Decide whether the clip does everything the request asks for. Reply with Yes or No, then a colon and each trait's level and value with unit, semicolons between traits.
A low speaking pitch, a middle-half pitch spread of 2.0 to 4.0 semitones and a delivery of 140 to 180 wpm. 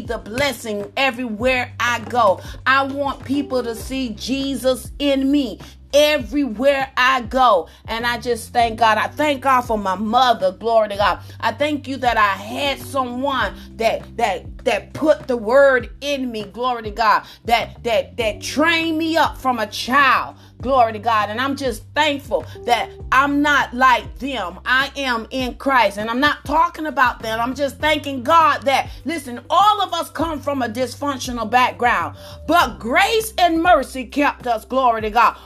No: very high, 265 Hz; average, 3.3 semitones; average, 175 wpm